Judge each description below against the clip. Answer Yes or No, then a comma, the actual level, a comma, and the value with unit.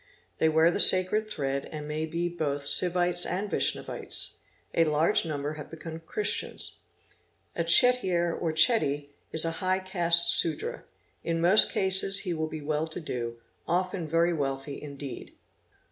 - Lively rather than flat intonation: No, average, 3.0 semitones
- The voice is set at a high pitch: No, medium, 165 Hz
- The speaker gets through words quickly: No, average, 150 wpm